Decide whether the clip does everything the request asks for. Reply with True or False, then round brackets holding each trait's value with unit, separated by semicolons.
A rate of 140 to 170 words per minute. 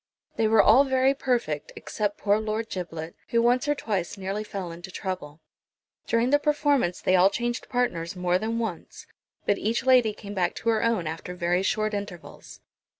False (180 wpm)